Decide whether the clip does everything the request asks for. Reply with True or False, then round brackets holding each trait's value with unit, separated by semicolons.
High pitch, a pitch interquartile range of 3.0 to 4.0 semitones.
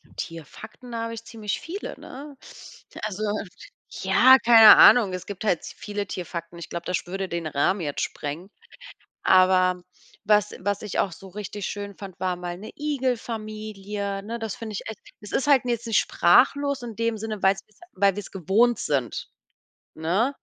True (205 Hz; 3.7 semitones)